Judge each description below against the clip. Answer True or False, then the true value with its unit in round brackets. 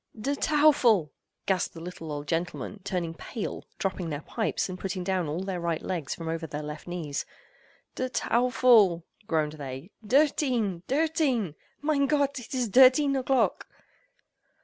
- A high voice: True (195 Hz)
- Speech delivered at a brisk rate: False (145 wpm)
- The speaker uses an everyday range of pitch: False (7.7 semitones)